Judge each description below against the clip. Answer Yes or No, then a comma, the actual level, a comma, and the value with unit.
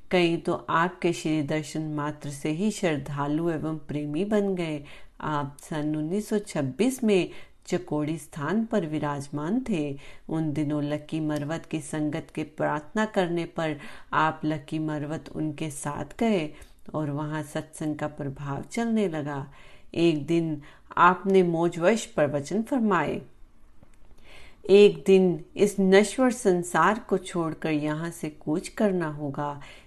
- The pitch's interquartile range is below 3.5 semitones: No, average, 3.9 semitones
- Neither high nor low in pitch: Yes, medium, 160 Hz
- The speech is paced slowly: No, average, 120 wpm